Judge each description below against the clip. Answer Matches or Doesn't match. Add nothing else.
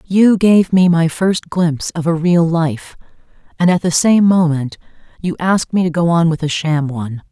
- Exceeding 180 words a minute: Matches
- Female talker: Matches